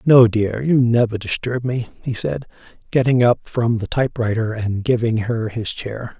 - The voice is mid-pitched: No, low, 120 Hz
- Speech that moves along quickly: No, average, 185 wpm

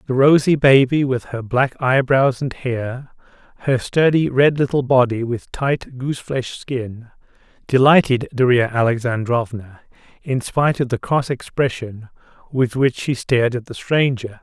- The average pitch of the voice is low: Yes, low, 125 Hz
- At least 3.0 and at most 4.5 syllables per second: Yes, 4.4 syllables/s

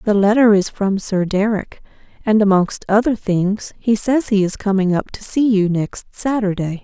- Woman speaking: Yes, female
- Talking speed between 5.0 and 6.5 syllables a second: No, 4.5 syllables/s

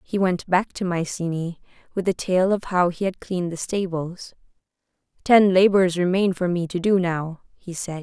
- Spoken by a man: No, female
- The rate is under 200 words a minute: Yes, average, 185 wpm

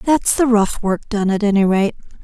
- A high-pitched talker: Yes, high, 215 Hz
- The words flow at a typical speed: No, fast, 215 wpm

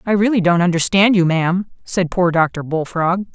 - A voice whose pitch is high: No, medium, 180 Hz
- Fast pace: No, average, 180 wpm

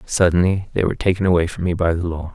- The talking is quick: Yes, fast, 255 wpm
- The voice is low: Yes, very low, 90 Hz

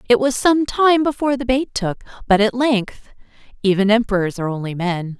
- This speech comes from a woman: Yes, female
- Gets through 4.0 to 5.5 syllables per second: Yes, 5.3 syllables/s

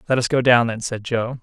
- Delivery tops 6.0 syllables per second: No, 5.6 syllables/s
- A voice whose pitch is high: No, low, 120 Hz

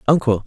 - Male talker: Yes, male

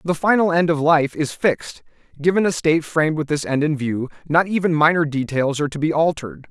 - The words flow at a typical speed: No, fast, 220 wpm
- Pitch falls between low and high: Yes, medium, 155 Hz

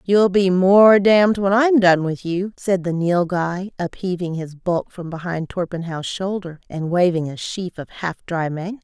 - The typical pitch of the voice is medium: Yes, medium, 180 Hz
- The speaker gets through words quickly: No, average, 185 wpm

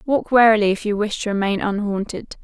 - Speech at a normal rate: Yes, average, 195 wpm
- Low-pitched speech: No, high, 210 Hz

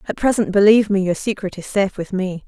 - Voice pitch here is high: Yes, high, 195 Hz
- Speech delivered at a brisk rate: Yes, fast, 240 wpm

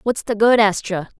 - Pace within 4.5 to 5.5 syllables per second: Yes, 5.0 syllables/s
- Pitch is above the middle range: Yes, high, 210 Hz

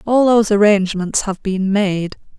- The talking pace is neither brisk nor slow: Yes, average, 150 wpm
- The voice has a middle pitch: No, high, 200 Hz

